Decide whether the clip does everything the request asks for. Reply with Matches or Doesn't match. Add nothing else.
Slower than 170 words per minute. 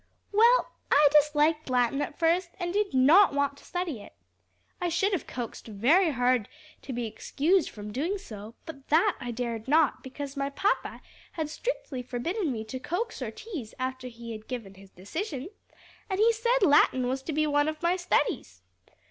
Doesn't match